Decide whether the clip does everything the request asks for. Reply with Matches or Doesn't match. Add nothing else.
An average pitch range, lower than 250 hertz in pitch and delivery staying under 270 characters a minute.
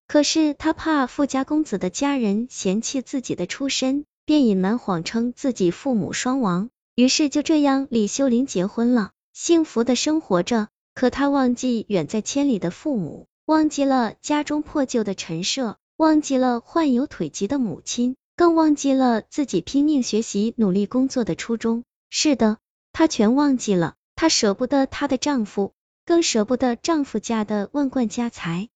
Doesn't match